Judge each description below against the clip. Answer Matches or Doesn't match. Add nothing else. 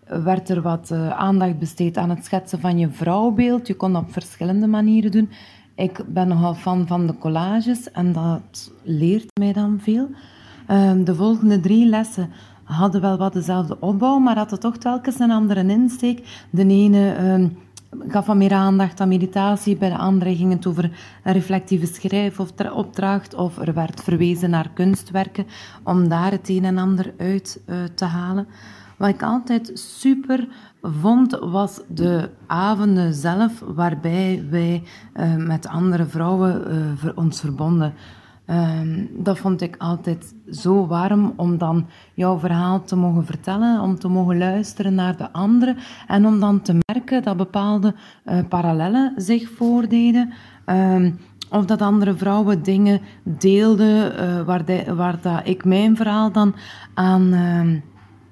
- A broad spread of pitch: Doesn't match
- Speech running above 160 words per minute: Doesn't match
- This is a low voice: Doesn't match